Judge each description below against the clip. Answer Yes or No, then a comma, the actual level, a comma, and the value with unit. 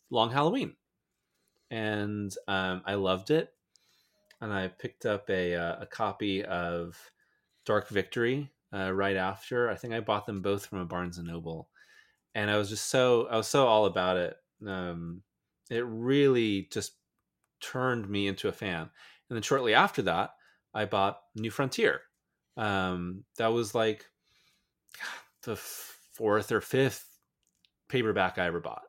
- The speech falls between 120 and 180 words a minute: Yes, average, 150 wpm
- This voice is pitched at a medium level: No, low, 100 Hz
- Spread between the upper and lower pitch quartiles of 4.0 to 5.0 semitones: No, average, 3.2 semitones